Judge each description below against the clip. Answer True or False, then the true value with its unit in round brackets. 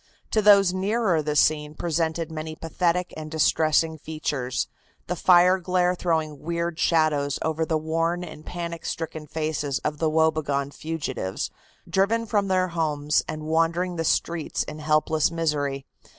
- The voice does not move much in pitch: True (2.2 semitones)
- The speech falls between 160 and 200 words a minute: False (150 wpm)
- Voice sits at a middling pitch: True (160 Hz)